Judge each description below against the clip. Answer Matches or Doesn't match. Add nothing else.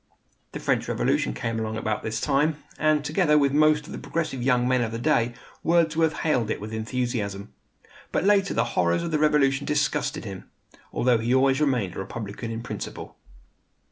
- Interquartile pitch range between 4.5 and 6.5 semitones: Matches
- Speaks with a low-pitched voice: Matches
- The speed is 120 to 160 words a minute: Doesn't match